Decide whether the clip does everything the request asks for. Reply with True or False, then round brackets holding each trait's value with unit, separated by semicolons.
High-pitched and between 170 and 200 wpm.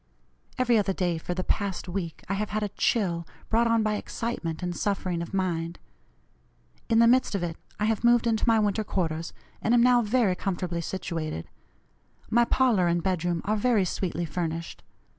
True (195 Hz; 180 wpm)